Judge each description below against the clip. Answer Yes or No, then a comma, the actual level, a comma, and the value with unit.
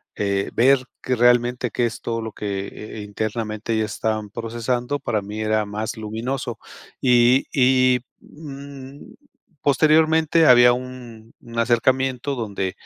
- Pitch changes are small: No, average, 3.0 semitones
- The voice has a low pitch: Yes, low, 120 Hz